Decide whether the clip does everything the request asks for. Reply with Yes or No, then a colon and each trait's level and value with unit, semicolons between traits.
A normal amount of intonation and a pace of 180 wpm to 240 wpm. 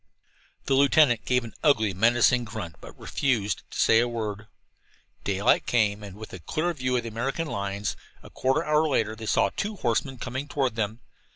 Yes: average, 4.0 semitones; average, 200 wpm